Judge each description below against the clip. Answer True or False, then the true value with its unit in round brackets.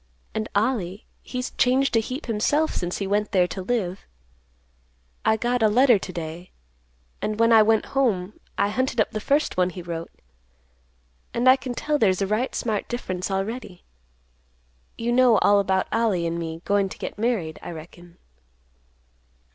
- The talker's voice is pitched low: False (210 Hz)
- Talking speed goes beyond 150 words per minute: True (170 wpm)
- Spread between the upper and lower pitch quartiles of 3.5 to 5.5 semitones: True (4.8 semitones)